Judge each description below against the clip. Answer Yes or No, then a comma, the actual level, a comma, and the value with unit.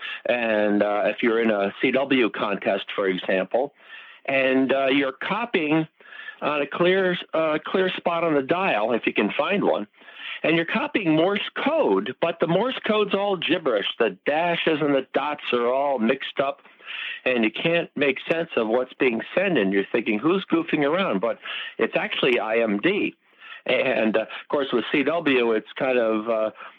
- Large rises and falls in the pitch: Yes, wide, 6.5 semitones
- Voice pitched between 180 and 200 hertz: No, medium, 140 Hz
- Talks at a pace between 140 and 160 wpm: No, average, 170 wpm